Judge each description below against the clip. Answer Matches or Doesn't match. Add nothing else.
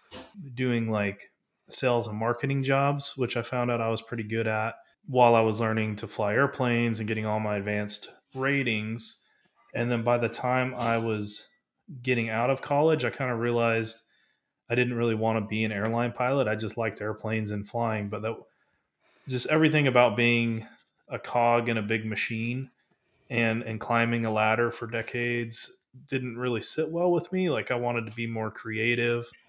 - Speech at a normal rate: Matches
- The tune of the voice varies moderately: Doesn't match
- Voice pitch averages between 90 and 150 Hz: Matches